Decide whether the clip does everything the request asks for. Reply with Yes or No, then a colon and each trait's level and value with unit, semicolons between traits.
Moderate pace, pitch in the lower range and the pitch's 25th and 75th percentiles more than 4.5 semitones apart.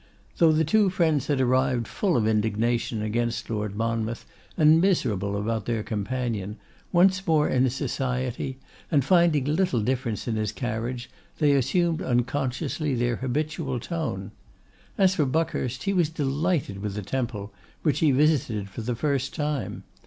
Yes: average, 150 wpm; low, 130 Hz; average, 5.2 semitones